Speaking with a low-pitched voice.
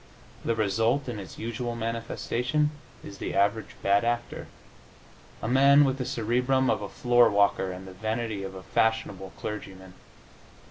Yes: low, 115 Hz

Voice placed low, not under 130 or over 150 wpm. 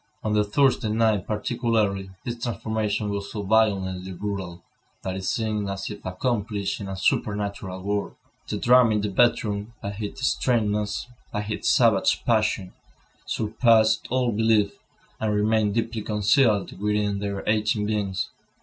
Yes: low, 105 Hz; average, 140 wpm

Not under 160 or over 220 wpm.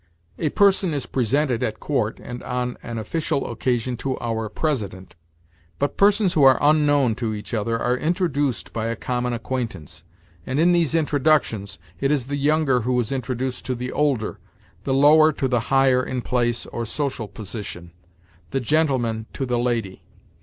Yes: average, 165 wpm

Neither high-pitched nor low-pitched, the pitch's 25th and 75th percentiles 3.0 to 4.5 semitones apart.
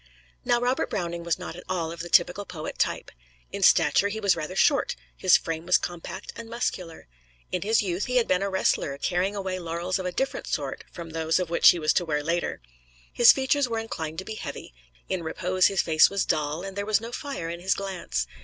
Yes: medium, 180 Hz; average, 3.3 semitones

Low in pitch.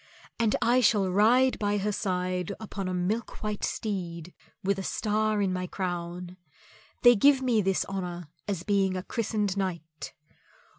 No: high, 195 Hz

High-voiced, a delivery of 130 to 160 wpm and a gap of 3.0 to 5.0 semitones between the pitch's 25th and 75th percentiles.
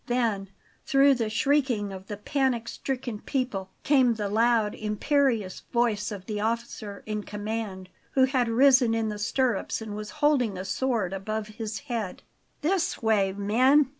Yes: high, 225 Hz; average, 155 wpm; average, 3.9 semitones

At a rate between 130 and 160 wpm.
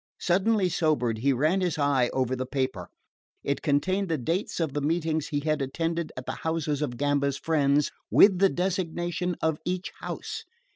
No: average, 175 wpm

